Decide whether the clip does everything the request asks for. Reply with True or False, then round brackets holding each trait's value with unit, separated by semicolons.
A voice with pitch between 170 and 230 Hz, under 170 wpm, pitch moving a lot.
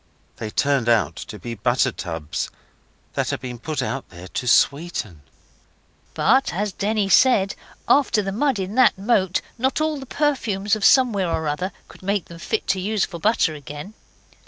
False (190 Hz; 175 wpm; 8.6 semitones)